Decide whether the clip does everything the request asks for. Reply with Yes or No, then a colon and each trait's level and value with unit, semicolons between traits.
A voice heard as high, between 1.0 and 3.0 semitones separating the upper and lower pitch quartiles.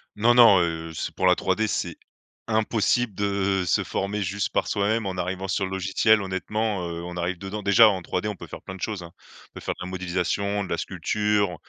No: very low, 95 Hz; narrow, 2.6 semitones